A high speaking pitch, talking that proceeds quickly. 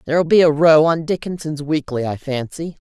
No: medium, 155 Hz; fast, 210 wpm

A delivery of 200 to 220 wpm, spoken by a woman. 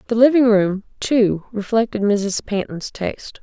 No: average, 140 wpm; female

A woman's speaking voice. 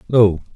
No: male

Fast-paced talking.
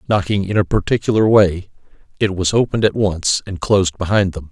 No: average, 185 wpm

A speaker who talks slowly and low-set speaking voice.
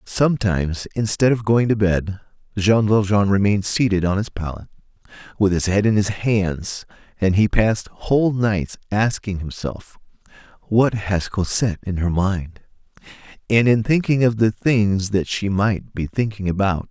No: average, 155 wpm; low, 100 Hz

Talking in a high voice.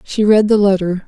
Yes: high, 200 Hz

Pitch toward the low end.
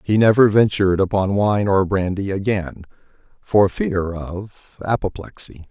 Yes: low, 100 Hz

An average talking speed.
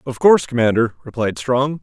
Yes: average, 165 wpm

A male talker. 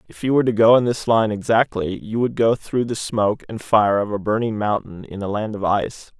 Yes: male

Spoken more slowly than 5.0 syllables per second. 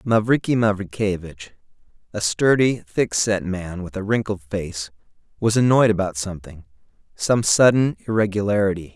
Yes: 4.8 syllables/s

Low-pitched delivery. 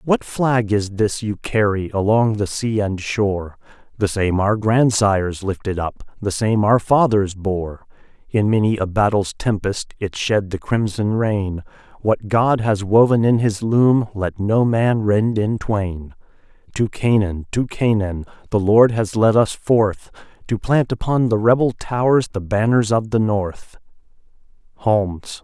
Yes: low, 105 Hz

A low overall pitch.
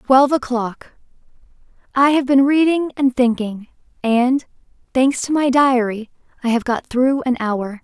No: very high, 255 Hz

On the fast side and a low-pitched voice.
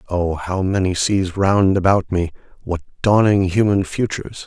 No: average, 150 wpm; very low, 95 Hz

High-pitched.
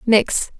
Yes: high, 220 Hz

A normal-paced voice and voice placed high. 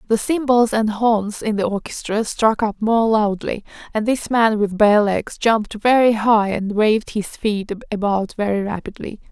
Yes: average, 175 wpm; high, 215 Hz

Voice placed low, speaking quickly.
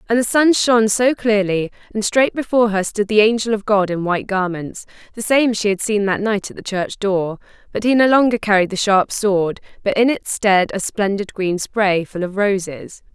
No: high, 205 Hz; fast, 220 wpm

